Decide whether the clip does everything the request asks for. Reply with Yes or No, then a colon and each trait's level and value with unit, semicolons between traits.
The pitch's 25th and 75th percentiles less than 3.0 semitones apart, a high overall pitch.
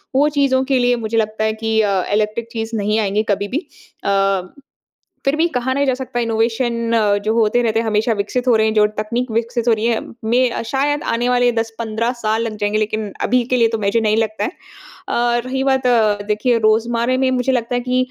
Yes: narrow, 2.5 semitones; high, 230 Hz